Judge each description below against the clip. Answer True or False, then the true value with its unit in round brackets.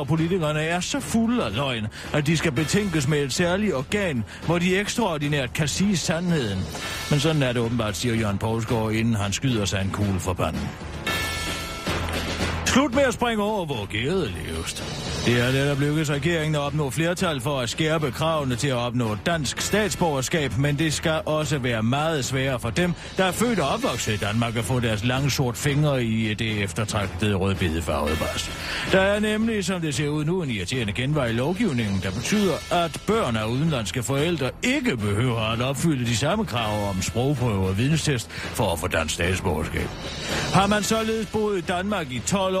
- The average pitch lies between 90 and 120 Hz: False (135 Hz)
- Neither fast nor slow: True (190 wpm)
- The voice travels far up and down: True (7.8 semitones)